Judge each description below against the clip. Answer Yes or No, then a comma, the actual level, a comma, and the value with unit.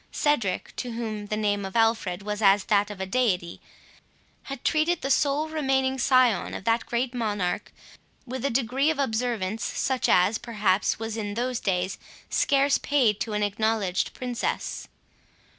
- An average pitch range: Yes, average, 4.2 semitones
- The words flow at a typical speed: Yes, average, 160 wpm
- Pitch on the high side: Yes, high, 225 Hz